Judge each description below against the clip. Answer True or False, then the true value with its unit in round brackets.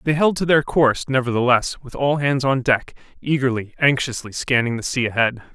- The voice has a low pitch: True (130 Hz)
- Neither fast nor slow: True (185 wpm)